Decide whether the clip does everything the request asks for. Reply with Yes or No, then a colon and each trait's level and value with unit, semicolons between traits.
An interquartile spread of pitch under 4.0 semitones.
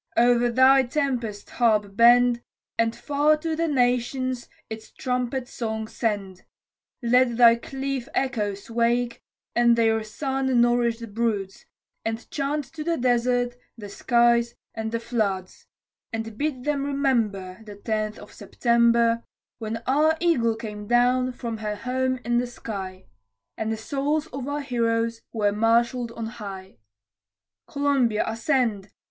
Yes: narrow, 2.6 semitones